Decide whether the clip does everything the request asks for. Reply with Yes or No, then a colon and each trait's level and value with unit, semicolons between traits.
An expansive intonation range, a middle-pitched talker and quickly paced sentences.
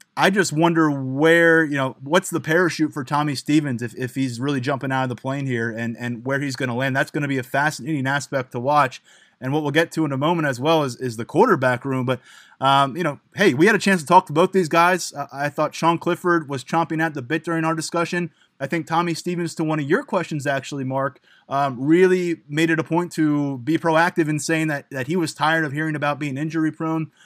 No: average, 3.3 semitones; medium, 155 Hz; fast, 250 wpm